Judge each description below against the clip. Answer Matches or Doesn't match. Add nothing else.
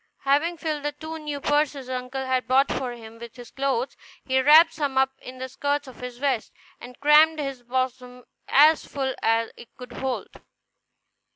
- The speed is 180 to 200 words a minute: Matches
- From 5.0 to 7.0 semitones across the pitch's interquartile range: Doesn't match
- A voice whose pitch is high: Matches